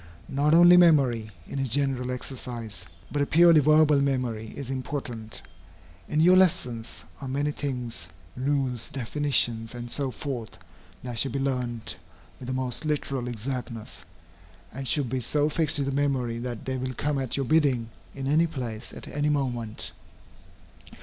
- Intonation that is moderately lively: Yes, average, 3.2 semitones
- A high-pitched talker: No, low, 135 Hz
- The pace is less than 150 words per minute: No, average, 155 wpm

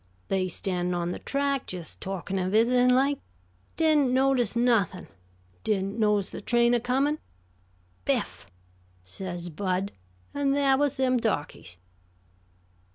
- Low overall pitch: No, high, 230 Hz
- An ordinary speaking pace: No, slow, 125 wpm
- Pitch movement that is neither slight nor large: No, wide, 6.1 semitones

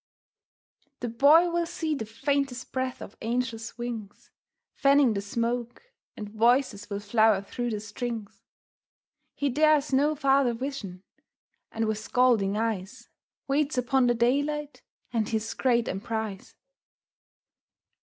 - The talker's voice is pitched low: No, high, 240 Hz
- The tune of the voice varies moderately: Yes, average, 4.1 semitones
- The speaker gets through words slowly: Yes, slow, 125 wpm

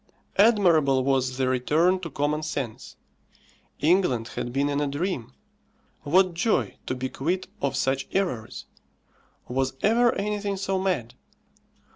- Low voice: No, medium, 150 Hz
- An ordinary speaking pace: No, slow, 130 wpm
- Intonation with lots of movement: Yes, wide, 6.2 semitones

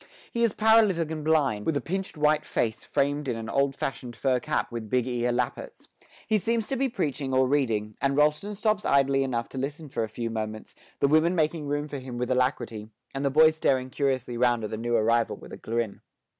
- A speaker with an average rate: No, fast, 220 wpm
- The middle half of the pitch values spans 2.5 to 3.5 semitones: No, average, 4.4 semitones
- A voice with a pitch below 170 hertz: Yes, low, 135 Hz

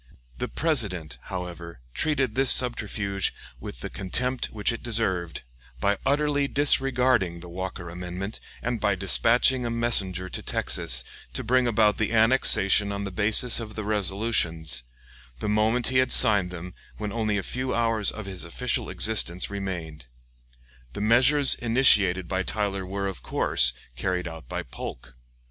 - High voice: No, low, 100 Hz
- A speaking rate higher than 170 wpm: No, average, 150 wpm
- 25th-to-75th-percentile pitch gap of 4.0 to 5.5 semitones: Yes, average, 4.6 semitones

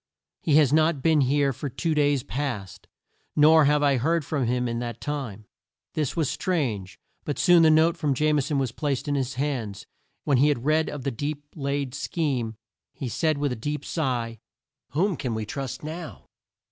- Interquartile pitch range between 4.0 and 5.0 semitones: No, average, 3.6 semitones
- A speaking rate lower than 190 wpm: No, average, 195 wpm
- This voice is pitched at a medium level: Yes, medium, 145 Hz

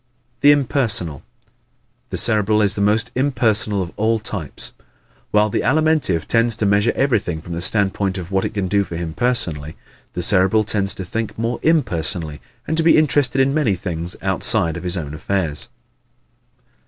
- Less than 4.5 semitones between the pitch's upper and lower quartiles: No, average, 5.0 semitones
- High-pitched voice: No, low, 100 Hz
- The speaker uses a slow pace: No, average, 175 wpm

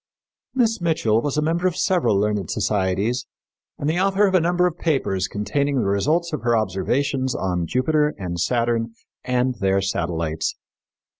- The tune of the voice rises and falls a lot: Yes, wide, 8.5 semitones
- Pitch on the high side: No, low, 125 Hz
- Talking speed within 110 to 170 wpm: Yes, average, 160 wpm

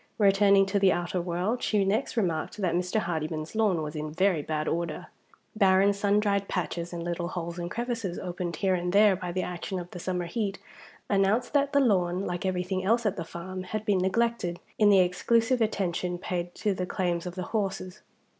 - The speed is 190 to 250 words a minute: Yes, average, 200 wpm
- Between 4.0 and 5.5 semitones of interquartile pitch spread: No, average, 2.8 semitones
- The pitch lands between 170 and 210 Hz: Yes, medium, 185 Hz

